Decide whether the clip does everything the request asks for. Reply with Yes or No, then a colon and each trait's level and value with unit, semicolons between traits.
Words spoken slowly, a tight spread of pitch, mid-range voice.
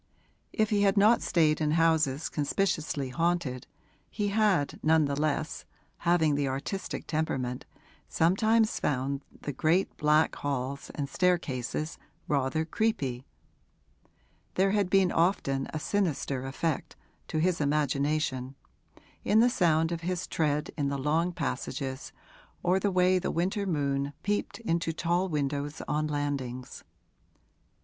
No: slow, 130 wpm; average, 4.4 semitones; medium, 155 Hz